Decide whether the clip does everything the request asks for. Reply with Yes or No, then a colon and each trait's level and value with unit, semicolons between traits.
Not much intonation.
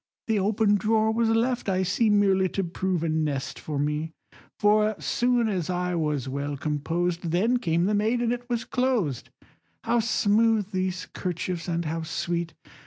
No: average, 4.9 semitones